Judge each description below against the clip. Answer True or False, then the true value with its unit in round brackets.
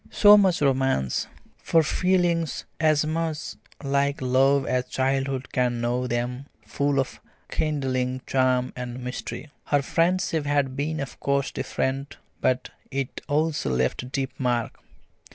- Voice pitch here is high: False (135 Hz)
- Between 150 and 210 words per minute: False (135 wpm)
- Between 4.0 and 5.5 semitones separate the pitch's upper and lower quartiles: False (2.9 semitones)